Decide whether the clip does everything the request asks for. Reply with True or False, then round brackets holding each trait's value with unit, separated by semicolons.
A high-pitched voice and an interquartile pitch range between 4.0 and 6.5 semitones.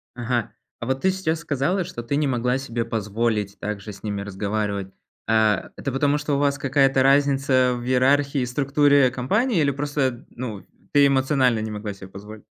False (130 Hz; 4.4 semitones)